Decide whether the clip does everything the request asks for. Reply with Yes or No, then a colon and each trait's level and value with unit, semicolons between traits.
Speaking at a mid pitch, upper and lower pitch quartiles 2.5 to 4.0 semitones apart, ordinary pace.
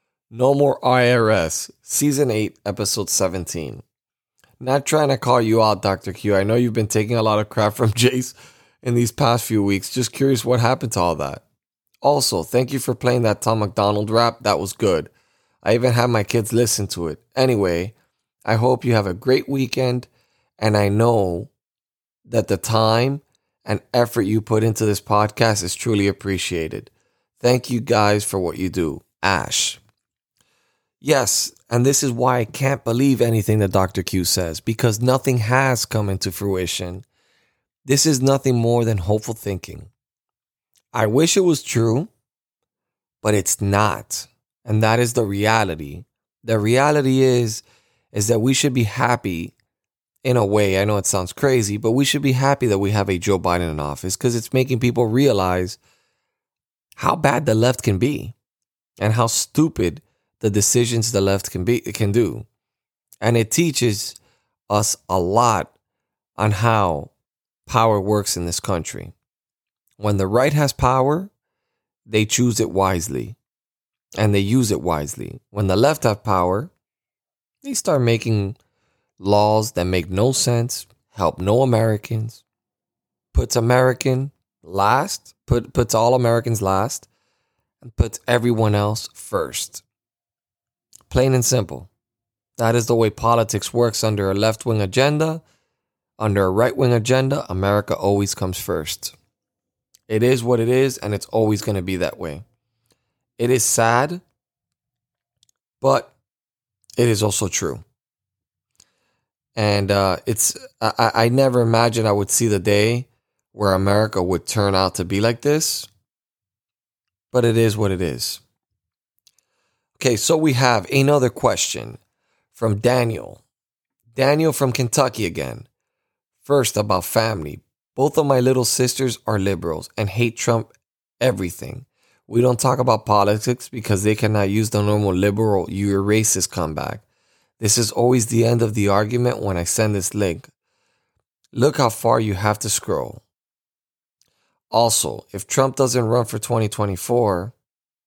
No: low, 115 Hz; average, 3.5 semitones; average, 150 wpm